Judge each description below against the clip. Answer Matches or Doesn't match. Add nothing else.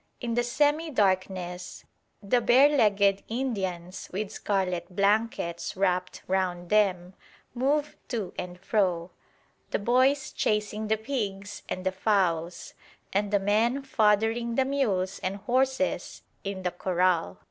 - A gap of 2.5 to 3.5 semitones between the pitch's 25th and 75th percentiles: Doesn't match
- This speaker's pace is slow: Matches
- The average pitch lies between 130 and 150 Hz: Doesn't match